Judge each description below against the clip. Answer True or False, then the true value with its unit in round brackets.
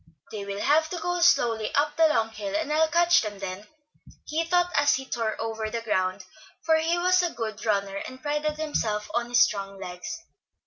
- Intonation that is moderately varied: False (7.0 semitones)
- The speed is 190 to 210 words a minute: True (205 wpm)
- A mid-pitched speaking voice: False (240 Hz)